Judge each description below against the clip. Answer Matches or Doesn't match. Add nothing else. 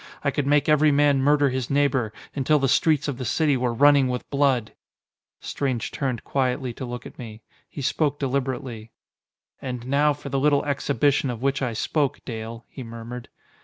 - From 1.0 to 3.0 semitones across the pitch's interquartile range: Matches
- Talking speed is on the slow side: Doesn't match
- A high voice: Doesn't match